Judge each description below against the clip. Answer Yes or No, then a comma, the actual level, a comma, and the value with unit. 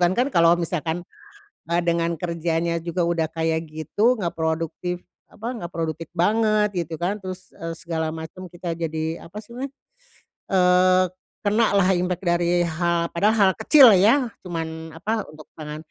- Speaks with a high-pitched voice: No, medium, 170 Hz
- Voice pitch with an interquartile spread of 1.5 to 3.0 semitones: Yes, narrow, 2.5 semitones